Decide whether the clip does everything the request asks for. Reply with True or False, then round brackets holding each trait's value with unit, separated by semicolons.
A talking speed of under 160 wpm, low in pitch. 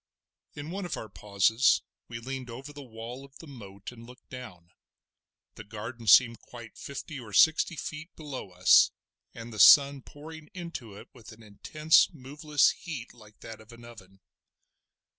False (165 wpm; 120 Hz)